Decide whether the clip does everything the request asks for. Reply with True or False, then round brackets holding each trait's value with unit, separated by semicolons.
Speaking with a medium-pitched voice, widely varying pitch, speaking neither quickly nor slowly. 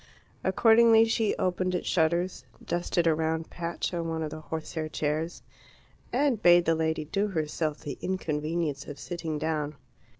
False (165 Hz; 2.5 semitones; 155 wpm)